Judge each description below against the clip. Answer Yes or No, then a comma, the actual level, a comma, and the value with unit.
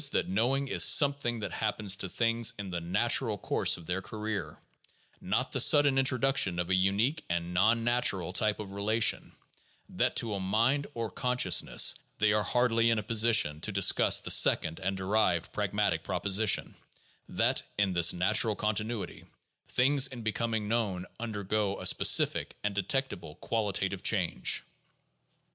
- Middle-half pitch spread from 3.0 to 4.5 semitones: Yes, average, 3.5 semitones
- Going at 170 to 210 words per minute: No, average, 155 wpm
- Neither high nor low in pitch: No, low, 105 Hz